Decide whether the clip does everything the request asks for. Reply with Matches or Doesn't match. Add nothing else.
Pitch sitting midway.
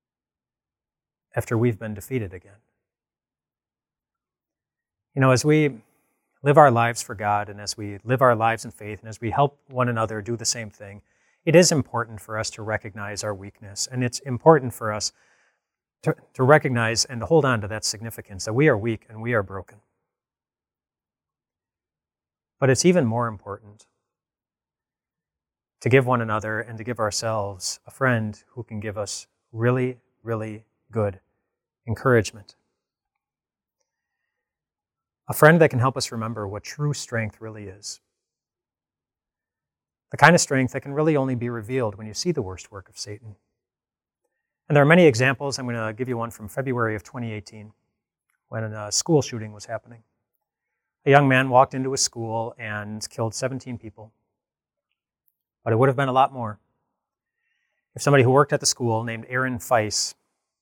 Doesn't match